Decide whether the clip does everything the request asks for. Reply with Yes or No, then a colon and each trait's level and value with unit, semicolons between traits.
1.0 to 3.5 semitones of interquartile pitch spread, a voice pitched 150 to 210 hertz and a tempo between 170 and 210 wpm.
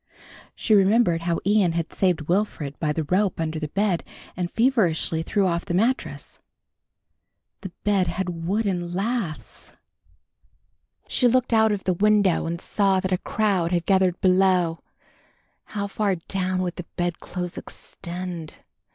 No: average, 3.0 semitones; medium, 185 Hz; average, 145 wpm